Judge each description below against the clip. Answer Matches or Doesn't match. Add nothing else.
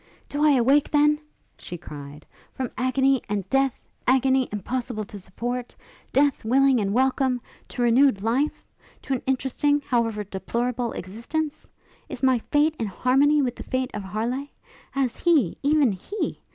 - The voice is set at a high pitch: Matches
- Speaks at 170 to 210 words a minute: Doesn't match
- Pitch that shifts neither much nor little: Matches